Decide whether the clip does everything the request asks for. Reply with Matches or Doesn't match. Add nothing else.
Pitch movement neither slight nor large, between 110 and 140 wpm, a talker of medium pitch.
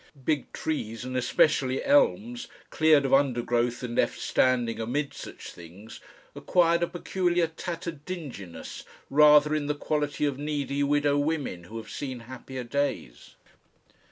Matches